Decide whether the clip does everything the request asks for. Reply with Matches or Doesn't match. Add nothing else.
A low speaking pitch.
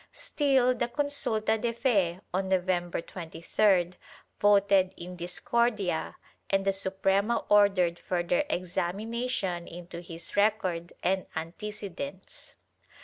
Doesn't match